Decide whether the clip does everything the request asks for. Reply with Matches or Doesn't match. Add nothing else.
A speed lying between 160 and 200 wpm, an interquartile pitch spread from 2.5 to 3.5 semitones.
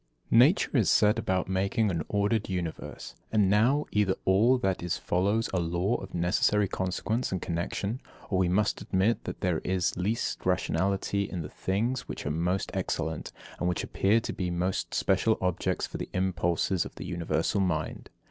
Matches